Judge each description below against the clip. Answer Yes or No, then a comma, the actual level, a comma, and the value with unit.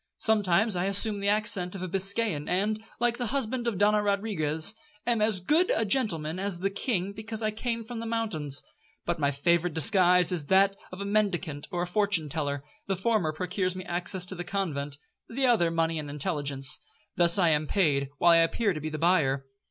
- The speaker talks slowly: No, average, 200 wpm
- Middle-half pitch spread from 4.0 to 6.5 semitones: Yes, average, 4.7 semitones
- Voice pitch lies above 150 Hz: Yes, medium, 185 Hz